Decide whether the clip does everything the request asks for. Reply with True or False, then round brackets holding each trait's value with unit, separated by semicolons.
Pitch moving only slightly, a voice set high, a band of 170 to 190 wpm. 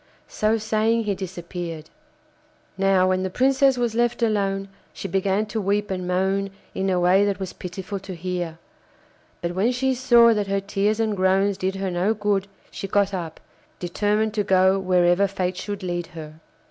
True (2.3 semitones; 195 Hz; 175 wpm)